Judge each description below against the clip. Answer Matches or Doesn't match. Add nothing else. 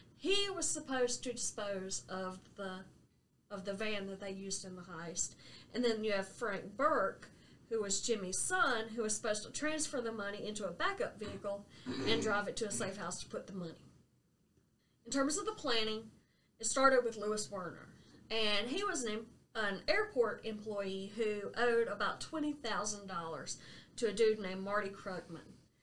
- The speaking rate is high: Doesn't match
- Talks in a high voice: Matches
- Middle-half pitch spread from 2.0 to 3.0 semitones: Doesn't match